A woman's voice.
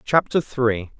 No: male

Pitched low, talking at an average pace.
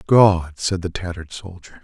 Yes: very low, 90 Hz; average, 165 wpm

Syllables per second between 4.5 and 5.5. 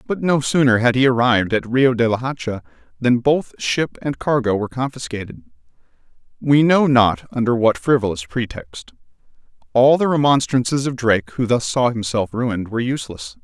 Yes: 5.4 syllables/s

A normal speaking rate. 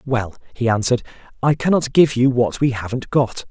Yes: average, 190 wpm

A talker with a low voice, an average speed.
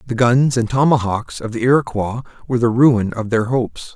Yes: low, 120 Hz; average, 195 wpm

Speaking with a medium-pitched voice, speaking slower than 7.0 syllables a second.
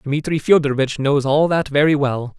Yes: medium, 145 Hz; 5.1 syllables/s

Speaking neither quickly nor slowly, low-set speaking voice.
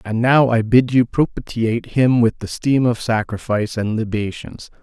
Yes: average, 175 wpm; low, 115 Hz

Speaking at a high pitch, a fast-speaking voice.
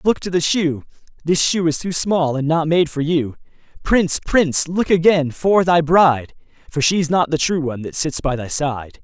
No: medium, 160 Hz; fast, 215 wpm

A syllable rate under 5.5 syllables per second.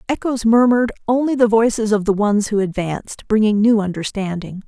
No: 5.6 syllables/s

